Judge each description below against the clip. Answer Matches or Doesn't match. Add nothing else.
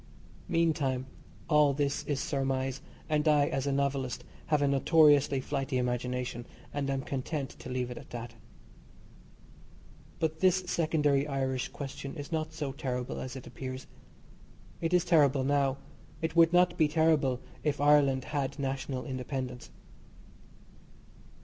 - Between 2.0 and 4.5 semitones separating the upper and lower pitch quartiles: Matches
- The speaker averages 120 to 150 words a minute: Matches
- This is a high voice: Doesn't match